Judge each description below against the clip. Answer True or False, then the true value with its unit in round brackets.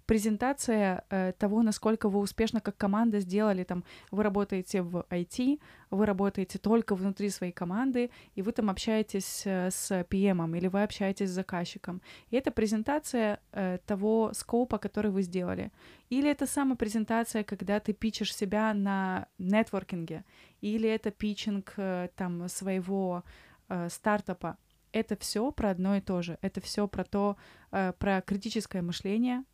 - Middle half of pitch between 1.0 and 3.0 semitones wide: True (2.6 semitones)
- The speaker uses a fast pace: False (150 wpm)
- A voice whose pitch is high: True (205 Hz)